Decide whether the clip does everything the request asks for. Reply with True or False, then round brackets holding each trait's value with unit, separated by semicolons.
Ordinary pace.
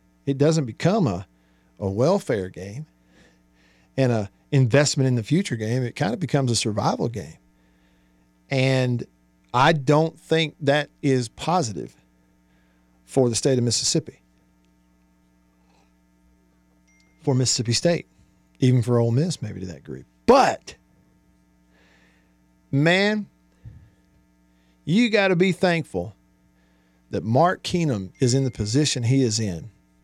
False (120 wpm)